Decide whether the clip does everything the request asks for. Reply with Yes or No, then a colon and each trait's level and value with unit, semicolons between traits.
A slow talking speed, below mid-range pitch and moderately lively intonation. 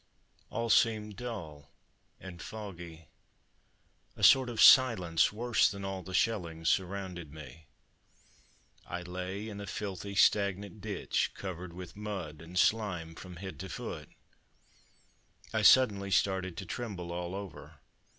Yes: slow, 130 wpm; very low, 95 Hz; average, 3.3 semitones